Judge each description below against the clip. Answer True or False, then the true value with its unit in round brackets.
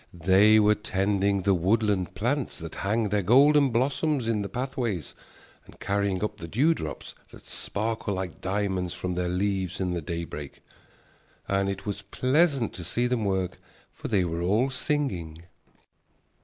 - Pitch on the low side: True (100 Hz)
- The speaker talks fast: False (155 wpm)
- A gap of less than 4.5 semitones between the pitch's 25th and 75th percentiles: True (4.1 semitones)